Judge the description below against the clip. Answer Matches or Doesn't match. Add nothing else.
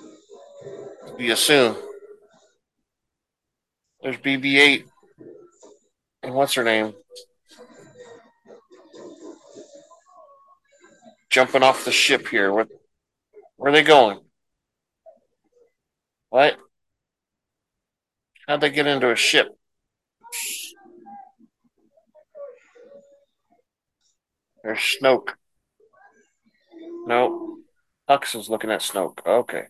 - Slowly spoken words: Matches